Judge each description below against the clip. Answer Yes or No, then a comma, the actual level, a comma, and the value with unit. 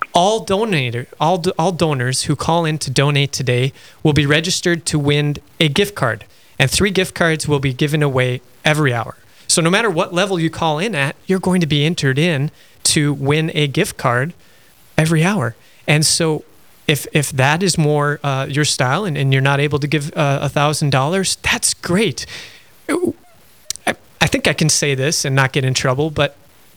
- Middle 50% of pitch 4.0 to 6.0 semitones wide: No, average, 3.0 semitones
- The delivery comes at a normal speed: Yes, average, 195 wpm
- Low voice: No, medium, 150 Hz